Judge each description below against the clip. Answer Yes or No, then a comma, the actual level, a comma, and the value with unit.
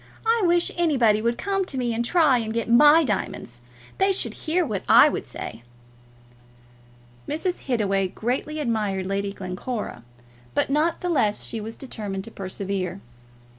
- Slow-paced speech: No, average, 155 wpm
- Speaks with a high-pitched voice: Yes, high, 235 Hz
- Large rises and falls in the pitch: Yes, wide, 7.5 semitones